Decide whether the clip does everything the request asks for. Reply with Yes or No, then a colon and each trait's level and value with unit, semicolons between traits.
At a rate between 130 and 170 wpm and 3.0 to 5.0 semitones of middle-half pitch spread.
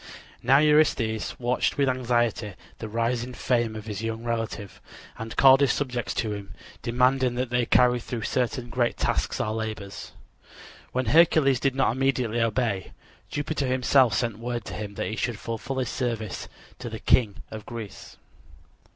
No: average, 160 wpm; narrow, 2.5 semitones